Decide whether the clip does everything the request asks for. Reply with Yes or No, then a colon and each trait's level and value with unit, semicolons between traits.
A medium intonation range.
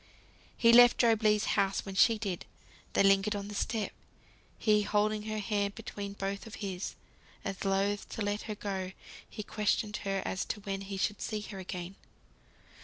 No: narrow, 1.5 semitones